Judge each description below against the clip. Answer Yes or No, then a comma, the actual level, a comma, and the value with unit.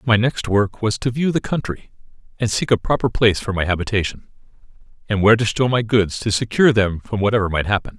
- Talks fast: Yes, fast, 220 wpm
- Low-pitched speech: Yes, low, 110 Hz